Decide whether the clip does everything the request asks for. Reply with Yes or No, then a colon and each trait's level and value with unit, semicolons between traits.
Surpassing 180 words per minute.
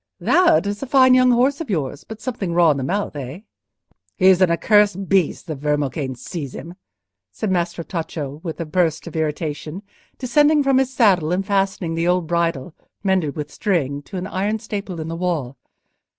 Yes: average, 190 wpm